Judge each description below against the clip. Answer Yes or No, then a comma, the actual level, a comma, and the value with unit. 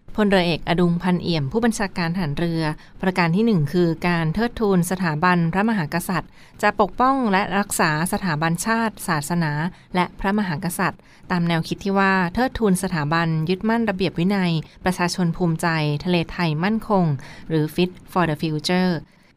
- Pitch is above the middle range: No, medium, 180 Hz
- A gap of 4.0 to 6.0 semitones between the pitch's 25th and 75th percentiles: No, average, 3.0 semitones